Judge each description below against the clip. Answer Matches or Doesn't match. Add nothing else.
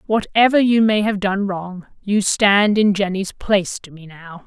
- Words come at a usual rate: Matches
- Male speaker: Doesn't match